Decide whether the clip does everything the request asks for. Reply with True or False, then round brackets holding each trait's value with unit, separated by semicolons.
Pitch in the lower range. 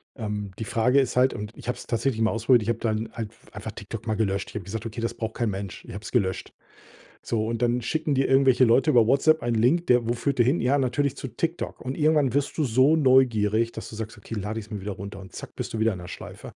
True (115 Hz)